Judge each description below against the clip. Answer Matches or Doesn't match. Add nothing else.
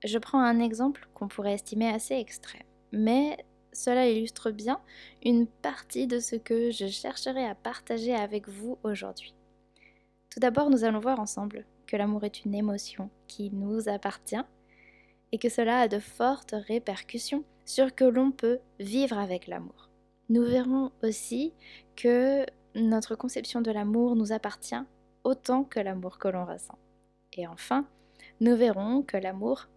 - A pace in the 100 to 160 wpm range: Matches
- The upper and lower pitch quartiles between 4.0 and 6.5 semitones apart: Doesn't match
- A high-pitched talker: Matches